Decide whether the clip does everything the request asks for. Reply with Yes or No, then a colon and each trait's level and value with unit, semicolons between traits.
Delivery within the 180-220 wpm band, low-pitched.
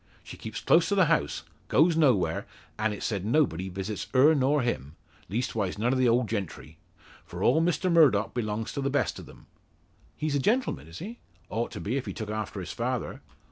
Yes: fast, 205 wpm; low, 120 Hz